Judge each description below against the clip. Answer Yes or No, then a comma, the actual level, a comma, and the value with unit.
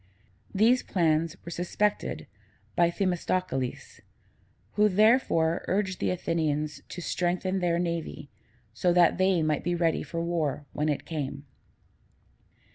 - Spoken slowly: Yes, slow, 120 wpm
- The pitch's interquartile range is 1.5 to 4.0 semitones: Yes, average, 2.9 semitones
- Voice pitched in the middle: Yes, medium, 170 Hz